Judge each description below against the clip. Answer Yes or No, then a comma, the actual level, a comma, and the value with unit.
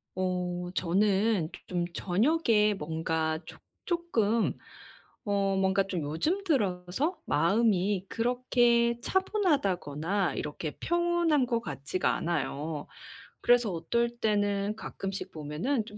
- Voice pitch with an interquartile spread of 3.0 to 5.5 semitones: Yes, average, 5.2 semitones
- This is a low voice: No, high, 200 Hz